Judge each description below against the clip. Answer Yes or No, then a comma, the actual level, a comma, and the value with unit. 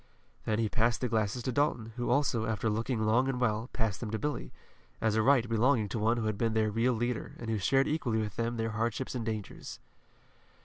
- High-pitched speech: No, low, 115 Hz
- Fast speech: Yes, fast, 225 wpm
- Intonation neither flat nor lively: No, narrow, 2.1 semitones